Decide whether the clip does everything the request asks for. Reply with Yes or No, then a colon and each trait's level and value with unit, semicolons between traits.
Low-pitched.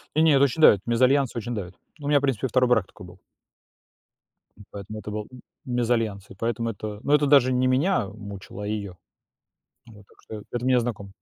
Yes: low, 115 Hz